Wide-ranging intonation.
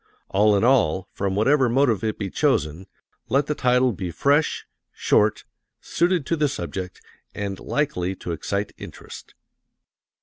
Yes: wide, 6.3 semitones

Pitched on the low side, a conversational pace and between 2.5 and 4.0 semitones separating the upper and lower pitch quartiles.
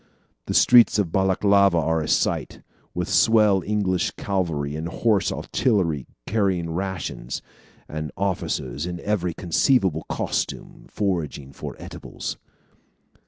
No: very low, 90 Hz; slow, 115 wpm; average, 3.7 semitones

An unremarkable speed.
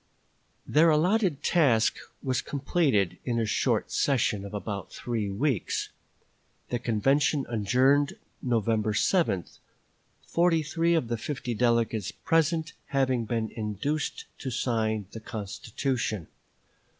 No: slow, 115 wpm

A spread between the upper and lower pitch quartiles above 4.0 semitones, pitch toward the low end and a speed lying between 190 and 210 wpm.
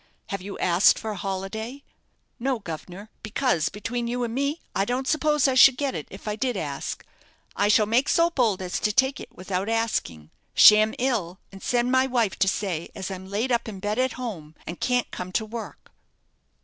No: average, 4.7 semitones; high, 220 Hz; average, 200 wpm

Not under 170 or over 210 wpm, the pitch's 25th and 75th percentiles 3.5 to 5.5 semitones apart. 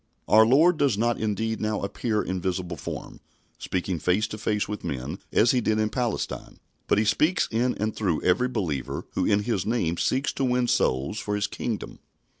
Yes: average, 195 wpm; average, 4.2 semitones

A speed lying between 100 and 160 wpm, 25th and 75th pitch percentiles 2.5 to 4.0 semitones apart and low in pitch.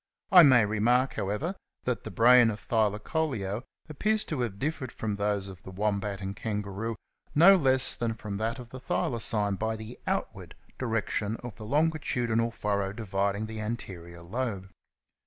Yes: average, 155 wpm; average, 3.7 semitones; low, 110 Hz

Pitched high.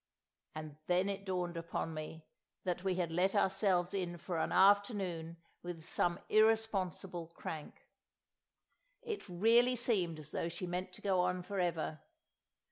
No: medium, 180 Hz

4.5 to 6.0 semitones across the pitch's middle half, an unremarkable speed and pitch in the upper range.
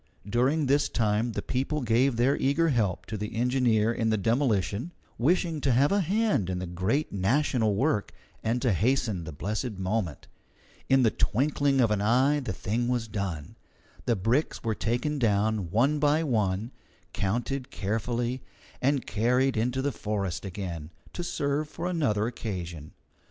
No: average, 4.9 semitones; average, 160 wpm; low, 115 Hz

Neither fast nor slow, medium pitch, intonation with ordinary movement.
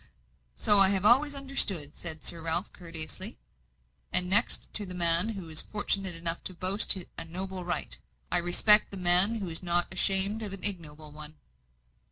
Yes: average, 175 wpm; medium, 180 Hz; average, 3.2 semitones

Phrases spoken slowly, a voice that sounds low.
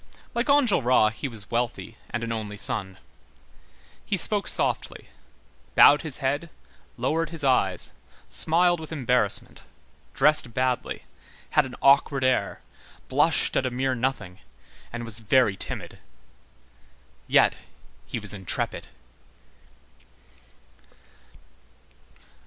Yes: slow, 105 wpm; low, 130 Hz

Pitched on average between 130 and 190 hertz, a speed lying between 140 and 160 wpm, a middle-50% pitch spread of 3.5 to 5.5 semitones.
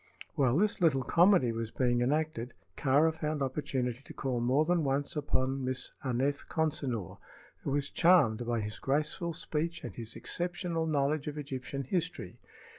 Yes: medium, 140 Hz; average, 155 wpm; average, 3.8 semitones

